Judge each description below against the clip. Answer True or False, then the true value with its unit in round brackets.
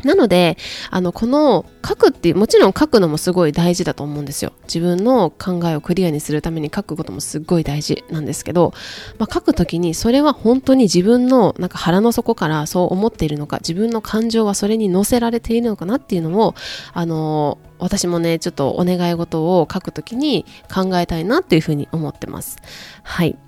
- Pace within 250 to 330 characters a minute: False (415 characters per minute)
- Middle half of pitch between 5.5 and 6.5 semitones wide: True (5.9 semitones)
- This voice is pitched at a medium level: True (180 Hz)